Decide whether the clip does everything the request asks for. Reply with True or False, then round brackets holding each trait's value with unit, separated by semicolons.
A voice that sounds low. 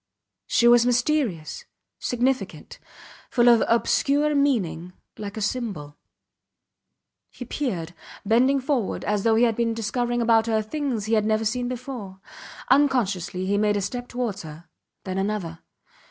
False (230 Hz)